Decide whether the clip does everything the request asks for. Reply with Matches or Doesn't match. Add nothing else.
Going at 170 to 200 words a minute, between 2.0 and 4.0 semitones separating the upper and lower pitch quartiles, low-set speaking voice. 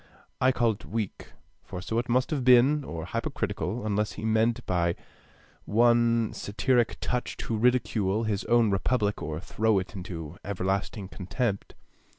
Doesn't match